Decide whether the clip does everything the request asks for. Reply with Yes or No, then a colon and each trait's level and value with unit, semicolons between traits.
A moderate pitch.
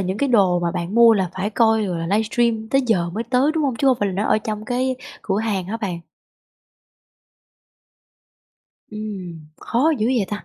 No: high, 215 Hz